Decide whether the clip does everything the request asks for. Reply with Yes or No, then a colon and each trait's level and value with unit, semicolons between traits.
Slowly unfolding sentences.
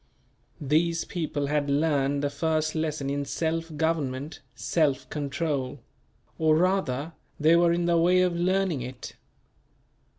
Yes: slow, 130 wpm